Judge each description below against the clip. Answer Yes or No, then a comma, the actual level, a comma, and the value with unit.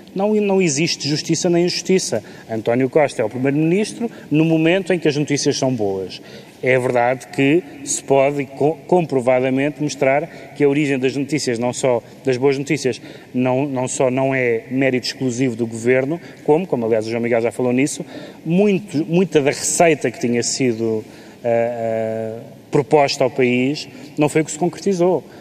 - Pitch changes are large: No, average, 4.0 semitones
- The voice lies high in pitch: No, medium, 140 Hz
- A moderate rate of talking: Yes, average, 170 wpm